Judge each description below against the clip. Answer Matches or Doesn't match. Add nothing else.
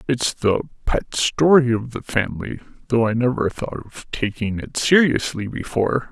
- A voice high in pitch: Doesn't match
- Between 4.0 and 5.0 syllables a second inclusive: Matches